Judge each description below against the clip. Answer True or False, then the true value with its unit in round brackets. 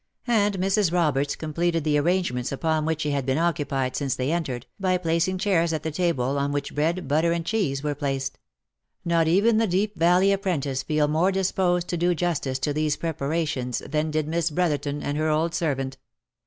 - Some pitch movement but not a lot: True (3.5 semitones)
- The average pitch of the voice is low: False (160 Hz)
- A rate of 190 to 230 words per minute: True (195 wpm)